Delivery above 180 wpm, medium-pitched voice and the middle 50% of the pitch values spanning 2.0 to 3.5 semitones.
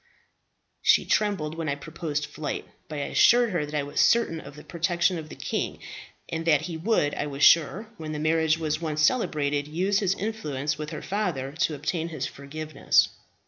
Yes: average, 190 wpm; medium, 155 Hz; narrow, 2.6 semitones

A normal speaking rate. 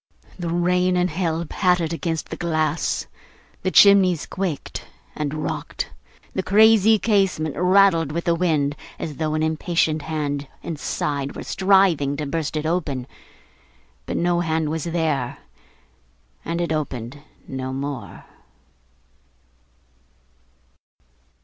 No: slow, 120 wpm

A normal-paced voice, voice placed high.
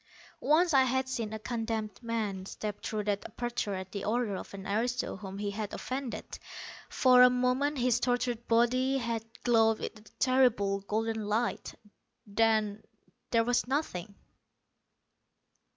Yes: average, 145 wpm; high, 230 Hz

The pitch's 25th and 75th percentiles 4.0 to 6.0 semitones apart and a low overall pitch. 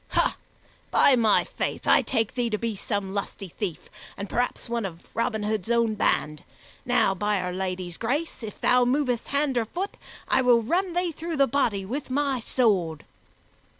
No: average, 4.7 semitones; high, 230 Hz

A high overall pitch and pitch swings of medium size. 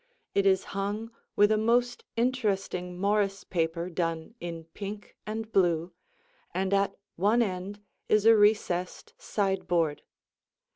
Yes: high, 195 Hz; average, 3.1 semitones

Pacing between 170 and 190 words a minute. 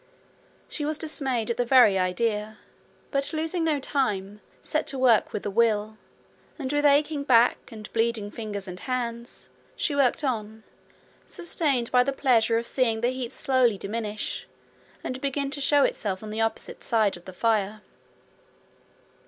No: average, 160 wpm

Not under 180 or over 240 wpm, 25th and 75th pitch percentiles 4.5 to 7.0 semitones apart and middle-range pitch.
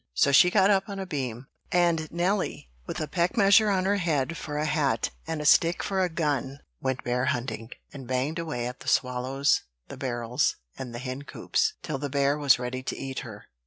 Yes: fast, 205 wpm; average, 5.1 semitones; medium, 145 Hz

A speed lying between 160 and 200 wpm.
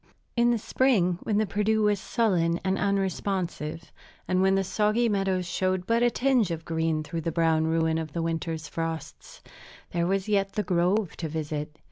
Yes: average, 180 wpm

